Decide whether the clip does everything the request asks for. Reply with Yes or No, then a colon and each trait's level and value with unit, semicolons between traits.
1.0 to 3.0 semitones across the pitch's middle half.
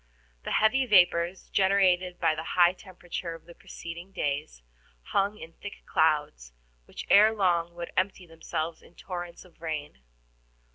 Yes: narrow, 2.6 semitones